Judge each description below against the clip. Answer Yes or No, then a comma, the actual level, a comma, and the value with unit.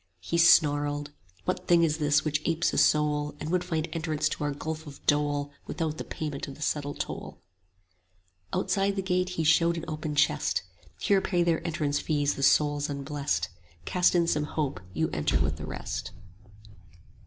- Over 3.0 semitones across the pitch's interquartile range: No, narrow, 2.4 semitones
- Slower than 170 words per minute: No, average, 185 wpm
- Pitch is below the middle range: No, medium, 150 Hz